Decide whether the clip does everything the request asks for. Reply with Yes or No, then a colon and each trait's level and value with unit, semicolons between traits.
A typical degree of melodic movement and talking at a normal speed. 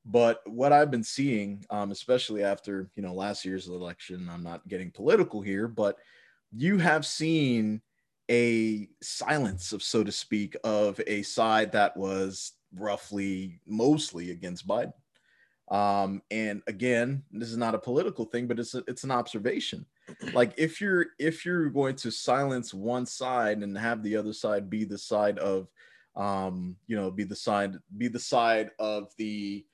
Yes: average, 3.4 semitones; average, 165 wpm